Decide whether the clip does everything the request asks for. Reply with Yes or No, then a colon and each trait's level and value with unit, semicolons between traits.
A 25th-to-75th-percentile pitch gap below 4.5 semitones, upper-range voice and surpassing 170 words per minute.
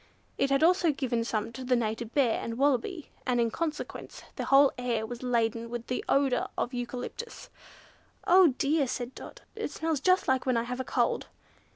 Yes: average, 3.4 semitones; very high, 255 Hz; average, 190 wpm